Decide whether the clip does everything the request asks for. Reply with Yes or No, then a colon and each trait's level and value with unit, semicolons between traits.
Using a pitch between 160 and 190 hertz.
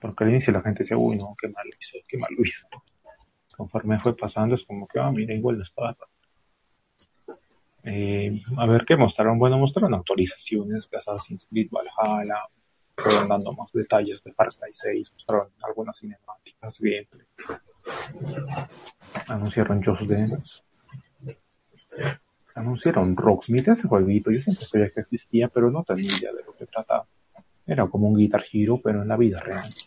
No: low, 110 Hz